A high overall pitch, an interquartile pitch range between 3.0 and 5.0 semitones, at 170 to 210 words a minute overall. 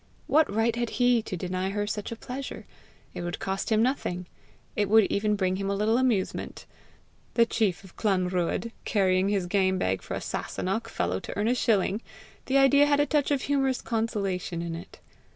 Yes: high, 210 Hz; average, 4.0 semitones; average, 190 wpm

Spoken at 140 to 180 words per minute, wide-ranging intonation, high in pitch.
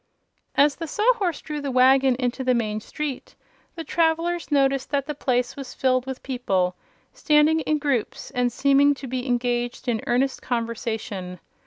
No: average, 160 wpm; average, 3.4 semitones; very high, 265 Hz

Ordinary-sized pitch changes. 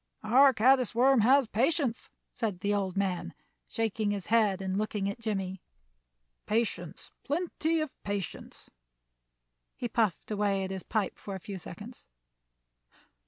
Yes: average, 3.8 semitones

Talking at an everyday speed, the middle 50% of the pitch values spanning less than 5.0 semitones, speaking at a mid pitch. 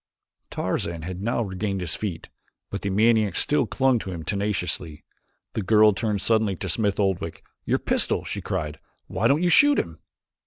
No: average, 170 wpm; average, 3.8 semitones; low, 100 Hz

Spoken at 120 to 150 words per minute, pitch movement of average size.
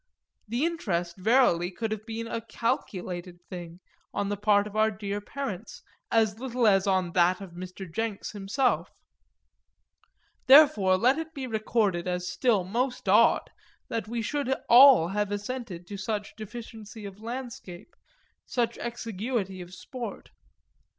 Yes: average, 140 wpm; average, 4.0 semitones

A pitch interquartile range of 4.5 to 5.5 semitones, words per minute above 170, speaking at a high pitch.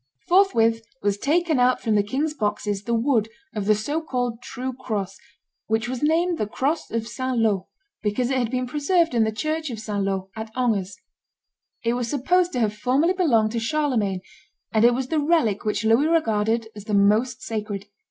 Yes: average, 4.8 semitones; average, 190 wpm; high, 235 Hz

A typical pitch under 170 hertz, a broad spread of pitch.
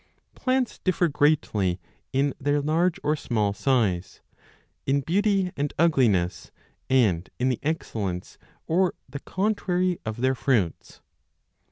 Yes: medium, 140 Hz; wide, 7.7 semitones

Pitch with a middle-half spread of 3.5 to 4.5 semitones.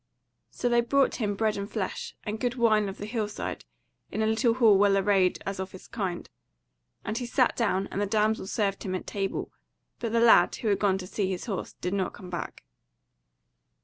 No: average, 2.7 semitones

